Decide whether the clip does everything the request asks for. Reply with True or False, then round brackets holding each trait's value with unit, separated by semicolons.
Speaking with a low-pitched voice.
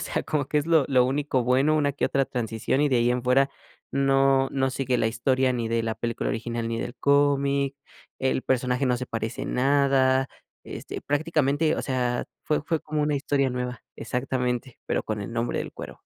True (130 Hz)